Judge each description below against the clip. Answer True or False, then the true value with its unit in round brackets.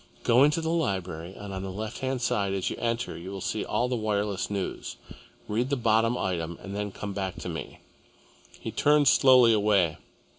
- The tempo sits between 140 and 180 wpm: False (195 wpm)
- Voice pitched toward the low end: True (105 Hz)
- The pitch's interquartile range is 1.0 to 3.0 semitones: False (4.1 semitones)